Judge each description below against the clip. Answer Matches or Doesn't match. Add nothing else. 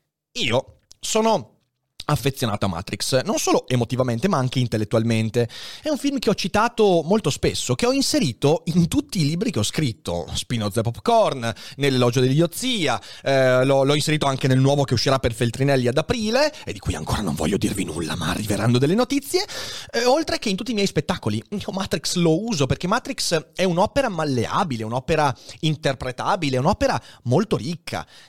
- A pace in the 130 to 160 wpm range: Doesn't match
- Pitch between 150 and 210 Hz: Doesn't match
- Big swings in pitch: Matches